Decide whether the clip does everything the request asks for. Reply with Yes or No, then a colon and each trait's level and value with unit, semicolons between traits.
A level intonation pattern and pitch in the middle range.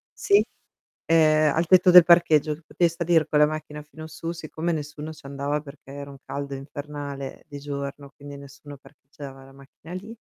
Yes: narrow, 2.3 semitones; medium, 150 Hz